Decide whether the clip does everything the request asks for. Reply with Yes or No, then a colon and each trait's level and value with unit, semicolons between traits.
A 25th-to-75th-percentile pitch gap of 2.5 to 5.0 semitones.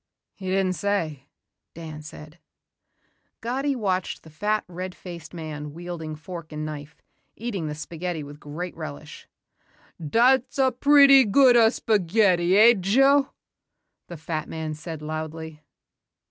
No: wide, 5.6 semitones